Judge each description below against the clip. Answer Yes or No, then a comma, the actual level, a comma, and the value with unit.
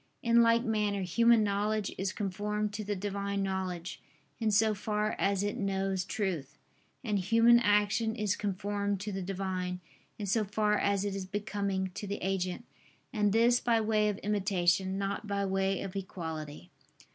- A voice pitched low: No, high, 200 Hz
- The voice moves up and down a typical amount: No, narrow, 1.7 semitones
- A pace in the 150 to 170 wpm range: Yes, average, 165 wpm